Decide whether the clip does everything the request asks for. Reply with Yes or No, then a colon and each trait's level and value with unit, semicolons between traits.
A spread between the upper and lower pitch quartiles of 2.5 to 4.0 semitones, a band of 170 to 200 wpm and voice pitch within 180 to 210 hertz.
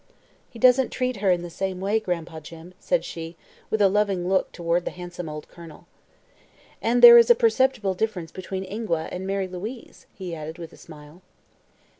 No: average, 4.4 semitones; average, 185 wpm; medium, 185 Hz